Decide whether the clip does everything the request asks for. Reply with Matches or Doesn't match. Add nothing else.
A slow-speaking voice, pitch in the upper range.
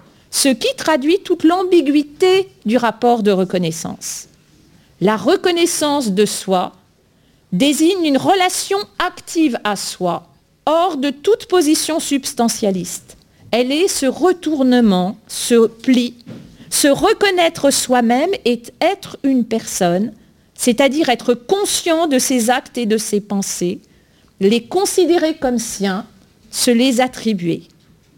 Matches